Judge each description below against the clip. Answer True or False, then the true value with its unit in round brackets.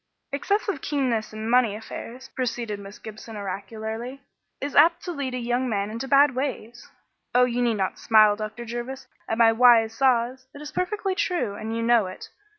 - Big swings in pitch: False (3.4 semitones)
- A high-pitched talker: True (240 Hz)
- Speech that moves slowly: False (180 wpm)